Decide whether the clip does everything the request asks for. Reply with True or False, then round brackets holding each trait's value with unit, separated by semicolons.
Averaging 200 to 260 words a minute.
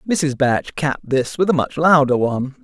True (205 wpm)